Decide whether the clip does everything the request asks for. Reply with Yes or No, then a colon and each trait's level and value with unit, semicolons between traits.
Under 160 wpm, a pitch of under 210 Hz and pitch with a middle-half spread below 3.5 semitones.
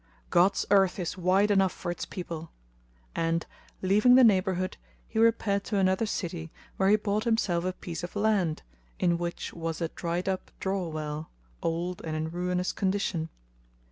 No: average, 165 wpm; medium, 185 Hz; average, 2.9 semitones